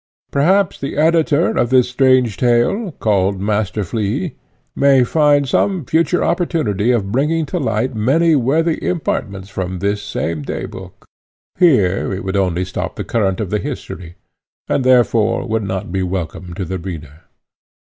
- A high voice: No, low, 115 Hz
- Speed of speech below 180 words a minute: Yes, average, 155 wpm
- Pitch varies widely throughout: Yes, wide, 7.1 semitones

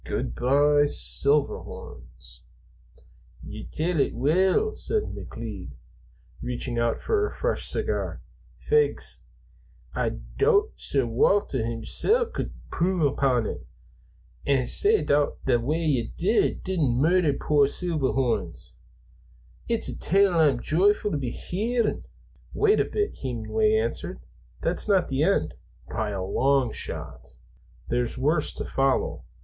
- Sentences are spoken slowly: Yes, slow, 120 wpm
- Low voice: No, medium, 145 Hz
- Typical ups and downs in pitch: No, wide, 8.0 semitones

